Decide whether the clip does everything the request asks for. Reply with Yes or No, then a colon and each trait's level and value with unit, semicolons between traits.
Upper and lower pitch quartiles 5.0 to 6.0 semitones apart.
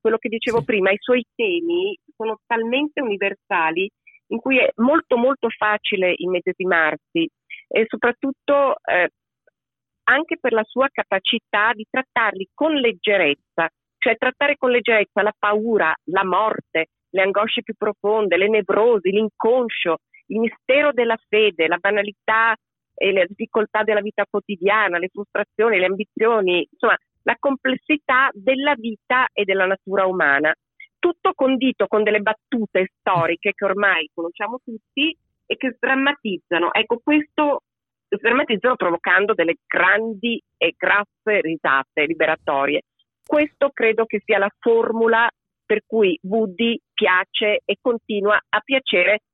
No: average, 4.4 semitones